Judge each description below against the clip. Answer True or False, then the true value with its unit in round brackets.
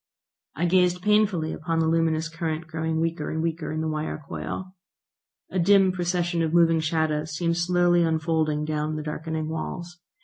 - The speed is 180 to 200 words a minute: False (165 wpm)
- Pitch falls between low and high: True (165 Hz)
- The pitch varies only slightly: True (1.8 semitones)